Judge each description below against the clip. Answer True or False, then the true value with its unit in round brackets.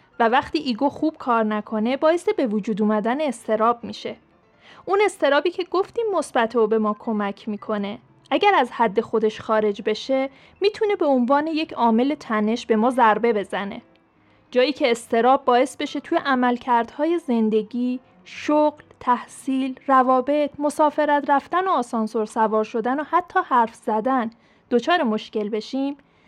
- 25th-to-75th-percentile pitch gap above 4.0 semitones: True (4.9 semitones)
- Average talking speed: True (140 wpm)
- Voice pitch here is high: True (250 Hz)